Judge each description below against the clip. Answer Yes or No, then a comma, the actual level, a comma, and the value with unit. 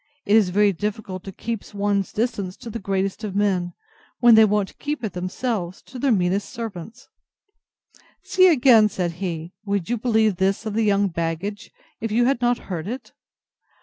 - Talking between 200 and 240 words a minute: No, average, 180 wpm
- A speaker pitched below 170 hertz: No, high, 205 Hz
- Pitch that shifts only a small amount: No, average, 3.4 semitones